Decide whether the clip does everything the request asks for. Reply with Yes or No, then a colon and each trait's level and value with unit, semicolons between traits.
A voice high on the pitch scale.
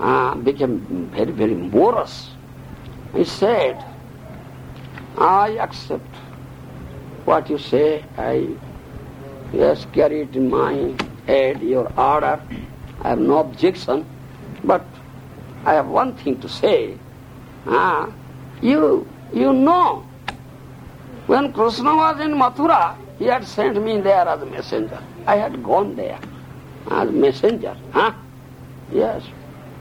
Yes: very high, 260 Hz